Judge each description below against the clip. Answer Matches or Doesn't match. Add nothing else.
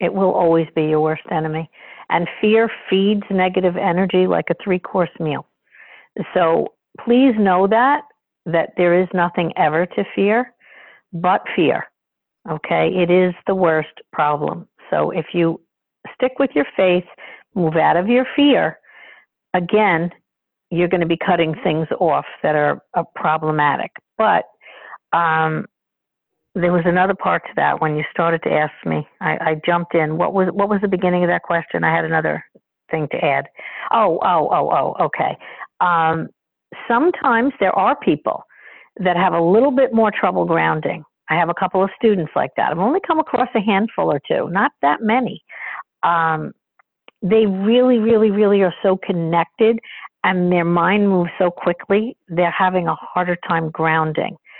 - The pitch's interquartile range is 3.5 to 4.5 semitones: Matches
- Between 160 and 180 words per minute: Matches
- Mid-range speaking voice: Matches